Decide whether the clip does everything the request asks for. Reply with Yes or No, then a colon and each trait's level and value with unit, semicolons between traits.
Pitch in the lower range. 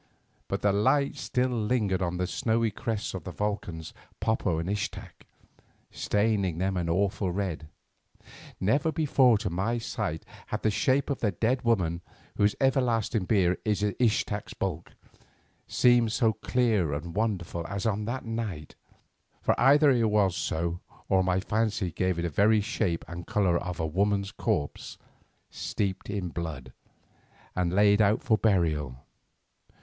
Yes: low, 100 Hz